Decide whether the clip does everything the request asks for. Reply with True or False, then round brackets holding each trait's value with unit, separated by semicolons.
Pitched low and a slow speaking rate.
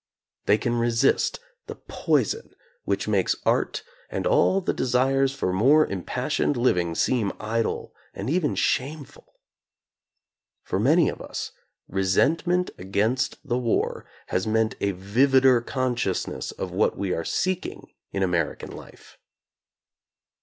True (120 Hz; 125 wpm)